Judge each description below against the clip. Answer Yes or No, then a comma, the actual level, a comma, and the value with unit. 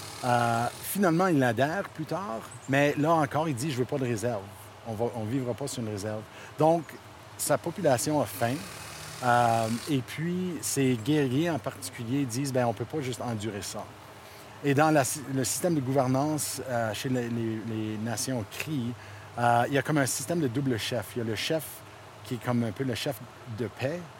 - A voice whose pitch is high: No, low, 125 Hz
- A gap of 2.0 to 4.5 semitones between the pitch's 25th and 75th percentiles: Yes, average, 4.2 semitones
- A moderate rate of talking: Yes, average, 200 wpm